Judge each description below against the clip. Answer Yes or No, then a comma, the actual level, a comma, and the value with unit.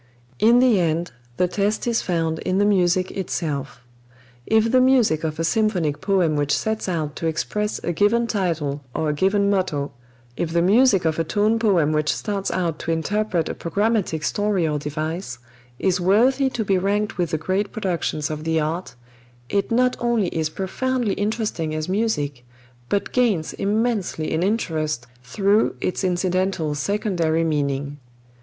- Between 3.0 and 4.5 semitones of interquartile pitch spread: No, average, 4.9 semitones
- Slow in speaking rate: No, average, 165 wpm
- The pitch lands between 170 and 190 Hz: Yes, medium, 185 Hz